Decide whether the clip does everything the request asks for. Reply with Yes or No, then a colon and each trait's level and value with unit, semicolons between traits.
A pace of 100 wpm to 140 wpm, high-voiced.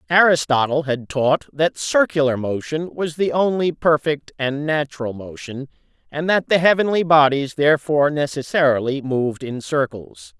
No: slow, 135 wpm; medium, 145 Hz